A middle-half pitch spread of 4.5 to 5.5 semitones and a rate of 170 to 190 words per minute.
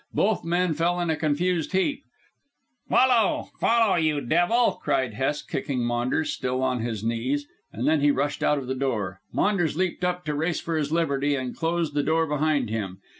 Yes: average, 4.8 semitones; average, 185 wpm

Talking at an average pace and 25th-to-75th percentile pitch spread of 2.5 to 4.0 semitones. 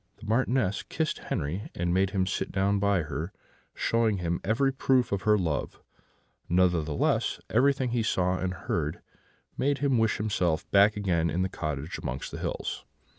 No: average, 165 wpm; average, 4.5 semitones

